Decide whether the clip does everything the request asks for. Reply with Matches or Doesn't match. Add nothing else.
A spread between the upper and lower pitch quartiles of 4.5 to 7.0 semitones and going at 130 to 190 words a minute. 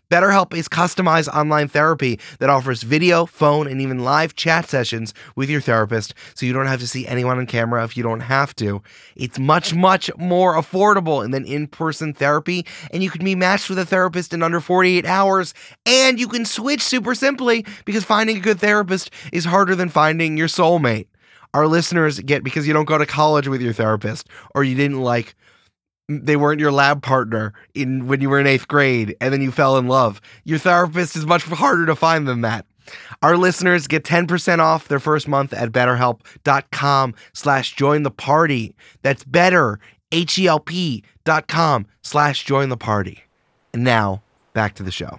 Matches